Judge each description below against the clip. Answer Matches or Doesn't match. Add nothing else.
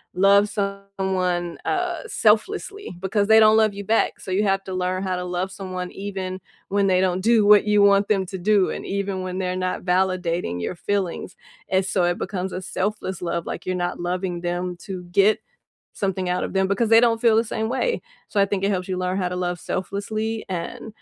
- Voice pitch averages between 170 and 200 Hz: Matches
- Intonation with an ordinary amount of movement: Doesn't match